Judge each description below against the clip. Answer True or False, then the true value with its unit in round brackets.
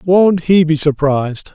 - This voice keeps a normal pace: True (155 wpm)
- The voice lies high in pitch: False (160 Hz)